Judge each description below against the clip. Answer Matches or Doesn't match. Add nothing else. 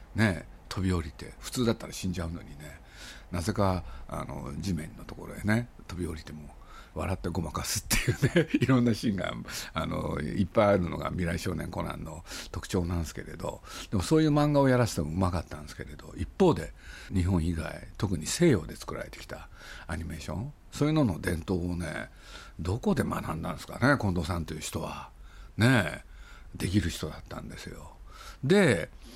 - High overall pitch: Doesn't match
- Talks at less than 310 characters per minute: Doesn't match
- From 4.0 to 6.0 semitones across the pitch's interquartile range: Matches